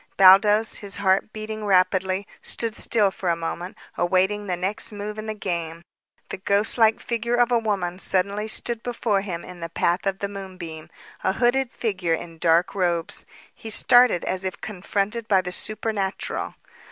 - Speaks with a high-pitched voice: Yes, high, 195 Hz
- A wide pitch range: No, average, 2.9 semitones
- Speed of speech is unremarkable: Yes, average, 170 wpm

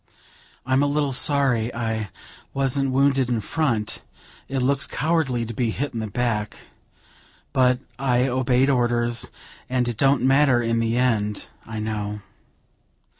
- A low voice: Yes, low, 125 Hz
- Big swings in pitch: No, average, 2.9 semitones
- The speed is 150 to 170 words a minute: No, average, 140 wpm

